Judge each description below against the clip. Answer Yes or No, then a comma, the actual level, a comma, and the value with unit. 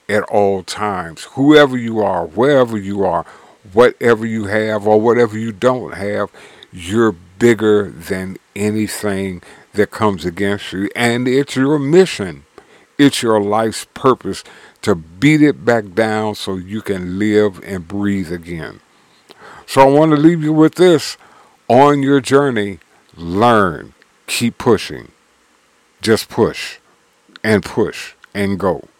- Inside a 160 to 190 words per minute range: No, slow, 135 wpm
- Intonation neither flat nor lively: Yes, average, 4.3 semitones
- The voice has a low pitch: Yes, low, 110 Hz